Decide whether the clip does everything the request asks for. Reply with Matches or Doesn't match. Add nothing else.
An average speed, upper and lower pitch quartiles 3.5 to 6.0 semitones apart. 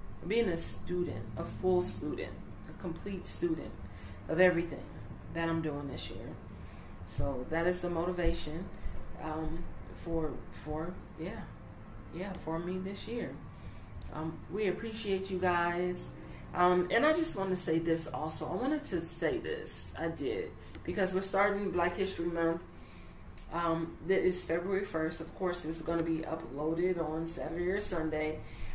Matches